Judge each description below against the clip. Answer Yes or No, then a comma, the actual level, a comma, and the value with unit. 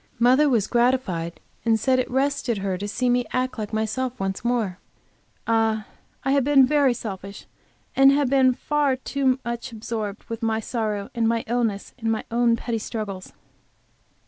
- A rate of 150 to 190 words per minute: Yes, average, 170 wpm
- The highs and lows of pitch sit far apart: No, average, 3.0 semitones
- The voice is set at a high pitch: Yes, high, 235 Hz